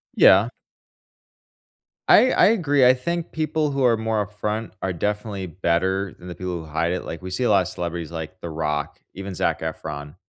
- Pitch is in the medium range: No, very low, 95 Hz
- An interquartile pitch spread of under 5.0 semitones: No, average, 5.3 semitones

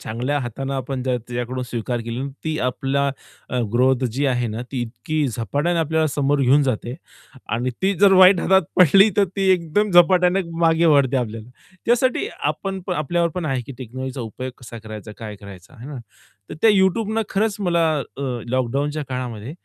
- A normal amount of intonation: No, wide, 5.9 semitones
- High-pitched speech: No, low, 135 Hz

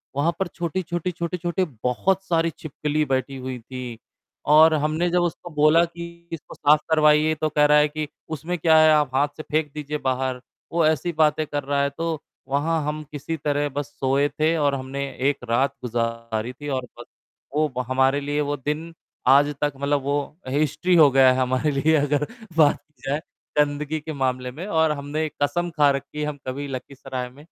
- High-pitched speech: No, medium, 150 Hz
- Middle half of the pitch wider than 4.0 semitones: No, narrow, 2.4 semitones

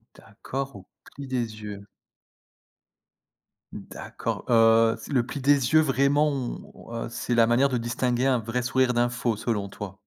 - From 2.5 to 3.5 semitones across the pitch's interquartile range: Yes, average, 2.9 semitones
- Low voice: Yes, low, 120 Hz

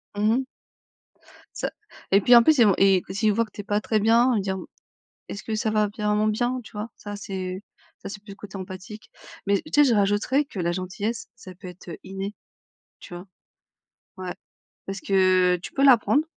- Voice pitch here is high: Yes, high, 205 Hz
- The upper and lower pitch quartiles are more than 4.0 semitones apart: No, average, 2.7 semitones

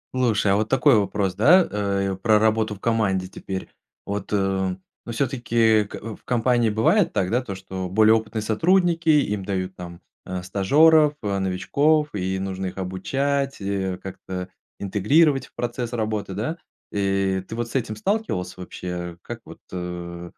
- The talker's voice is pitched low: Yes, low, 105 Hz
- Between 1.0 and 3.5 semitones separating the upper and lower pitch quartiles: No, average, 4.4 semitones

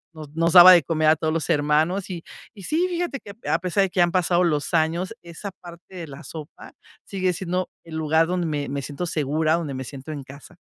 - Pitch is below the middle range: No, medium, 165 Hz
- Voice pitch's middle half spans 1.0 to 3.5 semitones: Yes, average, 2.8 semitones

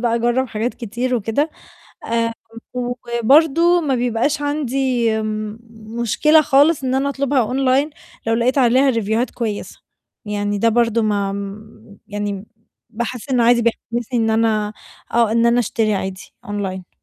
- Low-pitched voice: No, high, 235 Hz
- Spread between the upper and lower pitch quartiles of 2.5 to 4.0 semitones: Yes, average, 3.1 semitones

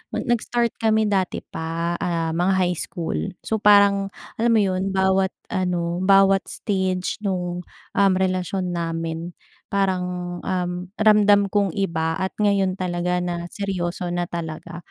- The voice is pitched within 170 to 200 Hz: Yes, medium, 185 Hz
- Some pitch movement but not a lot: No, narrow, 2.2 semitones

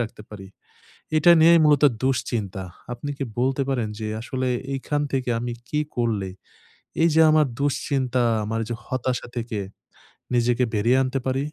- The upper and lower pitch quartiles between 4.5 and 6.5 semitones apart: No, average, 3.0 semitones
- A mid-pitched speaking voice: No, low, 130 Hz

